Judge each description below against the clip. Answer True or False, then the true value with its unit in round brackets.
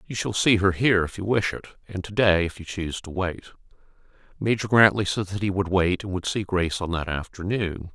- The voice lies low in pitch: True (95 Hz)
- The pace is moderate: False (225 wpm)